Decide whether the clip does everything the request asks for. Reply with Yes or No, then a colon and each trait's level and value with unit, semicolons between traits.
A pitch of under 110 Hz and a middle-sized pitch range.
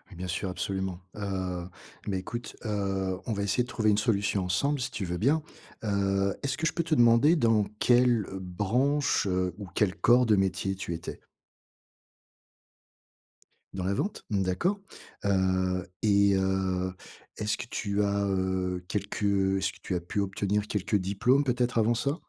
Yes: low, 100 Hz; average, 3.6 semitones